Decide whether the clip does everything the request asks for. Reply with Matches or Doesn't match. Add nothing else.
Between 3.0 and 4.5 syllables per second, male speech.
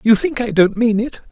Doesn't match